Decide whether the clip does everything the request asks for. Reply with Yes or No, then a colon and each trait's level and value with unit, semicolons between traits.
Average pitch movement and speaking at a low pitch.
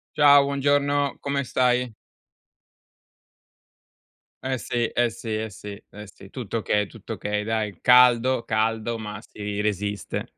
Yes: average, 3.7 semitones; low, 115 Hz